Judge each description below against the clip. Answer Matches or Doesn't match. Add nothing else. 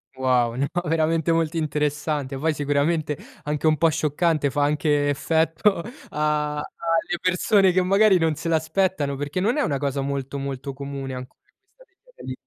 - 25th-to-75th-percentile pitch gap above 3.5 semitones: Doesn't match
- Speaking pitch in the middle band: Matches